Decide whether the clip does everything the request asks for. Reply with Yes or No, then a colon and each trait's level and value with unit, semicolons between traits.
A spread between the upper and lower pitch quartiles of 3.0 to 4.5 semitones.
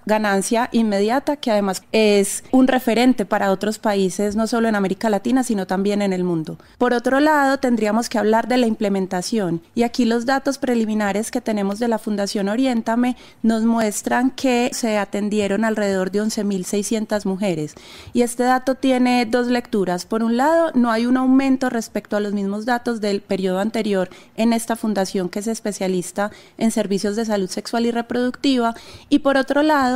Yes: average, 3.3 semitones